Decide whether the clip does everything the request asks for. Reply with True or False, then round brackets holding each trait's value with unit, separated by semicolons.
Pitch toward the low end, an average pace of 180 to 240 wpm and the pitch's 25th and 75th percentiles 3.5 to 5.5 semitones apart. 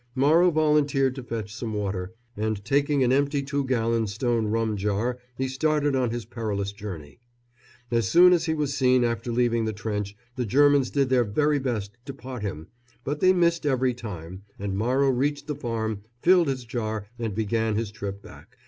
True (120 Hz; 185 wpm; 4.6 semitones)